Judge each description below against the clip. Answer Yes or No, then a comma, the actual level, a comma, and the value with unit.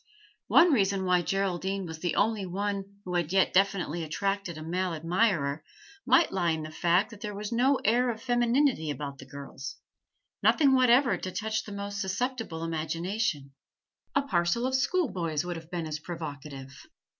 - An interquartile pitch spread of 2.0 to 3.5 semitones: No, average, 5.2 semitones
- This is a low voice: No, medium, 185 Hz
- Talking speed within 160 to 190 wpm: Yes, average, 165 wpm